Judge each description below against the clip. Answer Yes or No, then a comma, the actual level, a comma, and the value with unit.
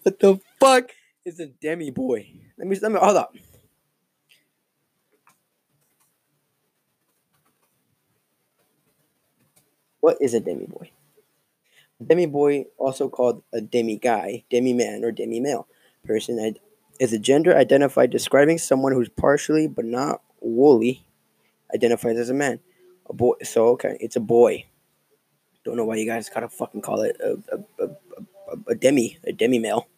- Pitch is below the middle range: No, medium, 145 Hz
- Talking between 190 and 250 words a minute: No, average, 145 wpm